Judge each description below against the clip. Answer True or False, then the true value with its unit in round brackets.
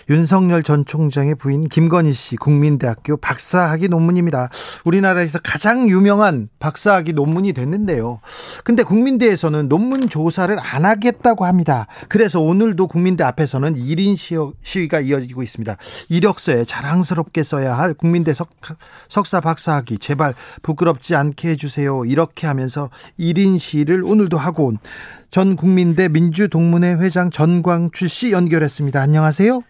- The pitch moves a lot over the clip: False (4.0 semitones)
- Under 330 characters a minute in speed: False (345 characters per minute)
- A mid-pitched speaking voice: True (165 Hz)